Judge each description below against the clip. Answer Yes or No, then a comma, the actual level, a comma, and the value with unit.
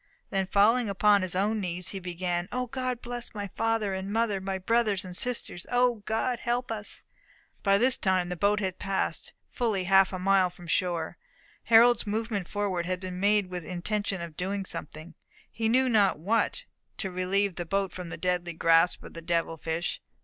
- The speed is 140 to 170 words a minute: No, average, 190 wpm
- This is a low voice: No, high, 195 Hz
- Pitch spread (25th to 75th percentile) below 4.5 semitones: Yes, average, 3.7 semitones